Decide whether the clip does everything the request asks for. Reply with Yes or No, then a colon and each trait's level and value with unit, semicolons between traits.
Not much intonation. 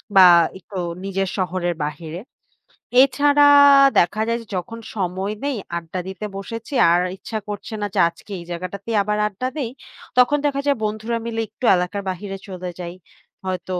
No: average, 4.0 semitones